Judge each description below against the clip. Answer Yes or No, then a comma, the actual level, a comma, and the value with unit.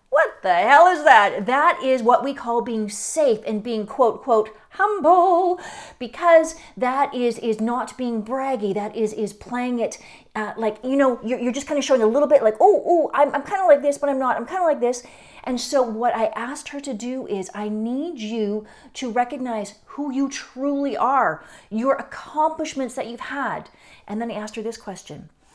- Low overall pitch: No, very high, 250 Hz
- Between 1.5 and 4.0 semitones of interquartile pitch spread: No, average, 4.5 semitones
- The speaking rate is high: Yes, fast, 210 wpm